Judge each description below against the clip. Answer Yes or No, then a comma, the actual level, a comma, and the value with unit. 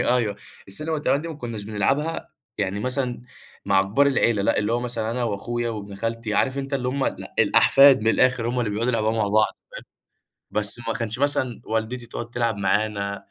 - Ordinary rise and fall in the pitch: Yes, average, 3.2 semitones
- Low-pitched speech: Yes, low, 115 Hz